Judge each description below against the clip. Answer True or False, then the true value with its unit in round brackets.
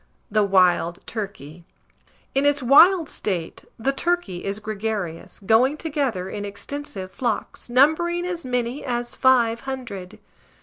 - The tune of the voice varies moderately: False (6.0 semitones)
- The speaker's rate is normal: False (125 wpm)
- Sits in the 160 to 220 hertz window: False (235 Hz)